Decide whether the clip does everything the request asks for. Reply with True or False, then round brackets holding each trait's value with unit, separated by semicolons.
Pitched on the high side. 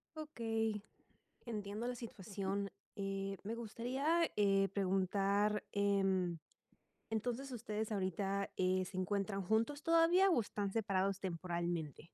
True (200 Hz)